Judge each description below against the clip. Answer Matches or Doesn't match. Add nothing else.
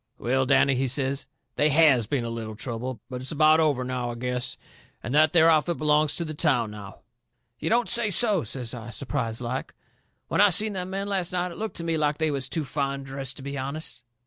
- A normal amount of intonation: Matches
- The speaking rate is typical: Doesn't match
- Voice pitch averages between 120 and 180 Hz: Matches